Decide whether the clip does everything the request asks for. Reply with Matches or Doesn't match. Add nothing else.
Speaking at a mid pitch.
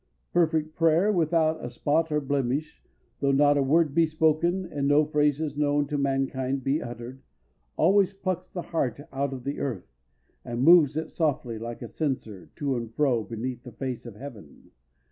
Matches